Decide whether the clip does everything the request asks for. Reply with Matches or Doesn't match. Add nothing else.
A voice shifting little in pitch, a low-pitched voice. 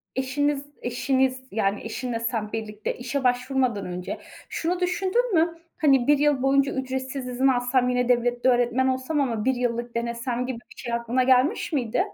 Doesn't match